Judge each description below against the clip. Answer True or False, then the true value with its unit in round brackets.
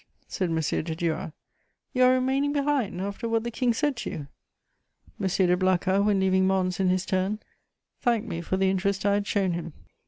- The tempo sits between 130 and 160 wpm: False (195 wpm)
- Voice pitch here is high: True (195 Hz)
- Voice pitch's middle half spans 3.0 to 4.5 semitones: True (4.0 semitones)